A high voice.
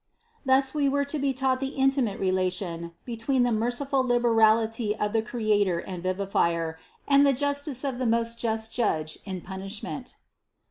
Yes: high, 230 Hz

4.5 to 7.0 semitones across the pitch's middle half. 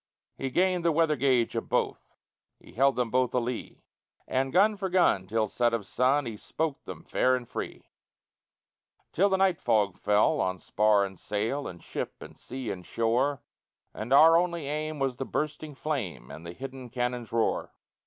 Yes: average, 5.2 semitones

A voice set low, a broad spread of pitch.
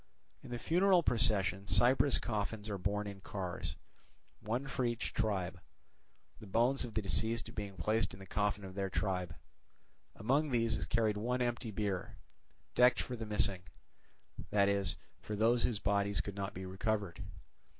No: low, 105 Hz; average, 3.2 semitones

